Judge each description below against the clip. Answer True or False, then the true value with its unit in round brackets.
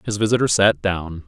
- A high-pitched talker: False (95 Hz)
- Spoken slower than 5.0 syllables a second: False (5.2 syllables/s)